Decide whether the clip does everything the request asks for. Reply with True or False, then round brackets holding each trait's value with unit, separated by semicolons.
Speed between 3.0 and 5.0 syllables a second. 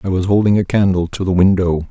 False (6.2 syllables/s)